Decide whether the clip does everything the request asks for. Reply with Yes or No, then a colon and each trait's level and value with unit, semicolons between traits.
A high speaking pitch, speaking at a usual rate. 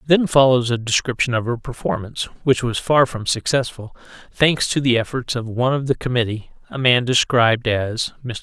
No: low, 125 Hz; average, 185 wpm